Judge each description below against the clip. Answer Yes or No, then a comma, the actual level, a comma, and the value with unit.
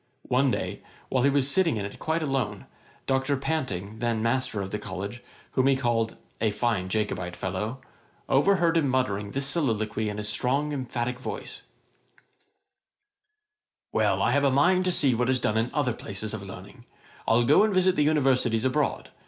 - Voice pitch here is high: No, low, 125 Hz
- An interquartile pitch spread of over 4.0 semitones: Yes, average, 4.7 semitones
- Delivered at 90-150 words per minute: No, average, 175 wpm